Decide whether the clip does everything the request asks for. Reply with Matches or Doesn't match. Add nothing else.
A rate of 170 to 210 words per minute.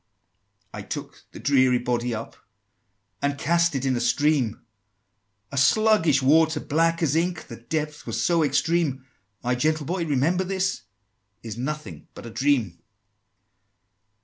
Doesn't match